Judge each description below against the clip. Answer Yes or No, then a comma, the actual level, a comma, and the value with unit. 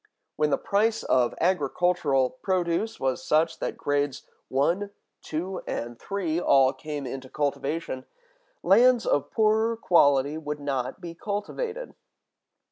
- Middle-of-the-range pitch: Yes, medium, 155 Hz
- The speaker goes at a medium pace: No, slow, 125 wpm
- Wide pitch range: Yes, wide, 6.2 semitones